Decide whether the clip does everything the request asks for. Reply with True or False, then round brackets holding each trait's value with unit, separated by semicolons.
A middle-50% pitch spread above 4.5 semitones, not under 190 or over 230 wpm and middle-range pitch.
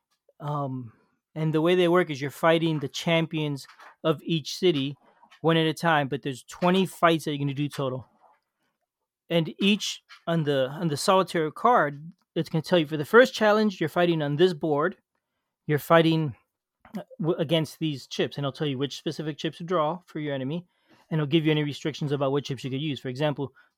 False (2.9 semitones; 205 wpm; 160 Hz)